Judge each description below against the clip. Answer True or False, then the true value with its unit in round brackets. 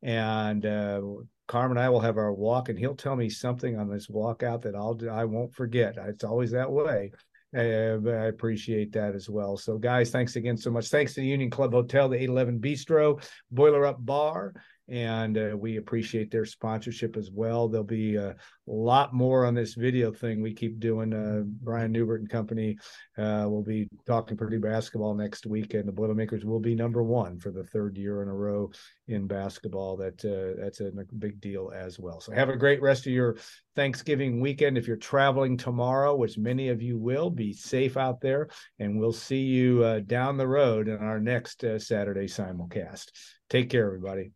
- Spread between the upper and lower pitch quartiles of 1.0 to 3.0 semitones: True (2.7 semitones)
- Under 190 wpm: False (200 wpm)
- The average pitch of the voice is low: True (115 Hz)